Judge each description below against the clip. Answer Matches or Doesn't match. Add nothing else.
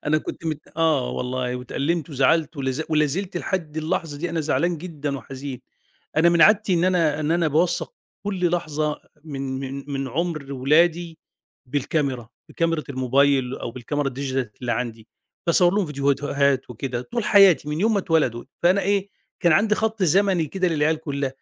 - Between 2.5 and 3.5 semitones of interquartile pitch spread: Doesn't match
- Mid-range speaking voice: Matches